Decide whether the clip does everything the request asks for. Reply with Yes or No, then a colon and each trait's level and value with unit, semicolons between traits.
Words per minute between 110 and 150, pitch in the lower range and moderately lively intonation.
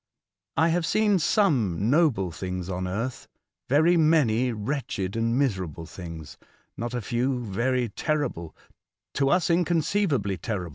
No: slow, 135 wpm; low, 120 Hz; wide, 8.3 semitones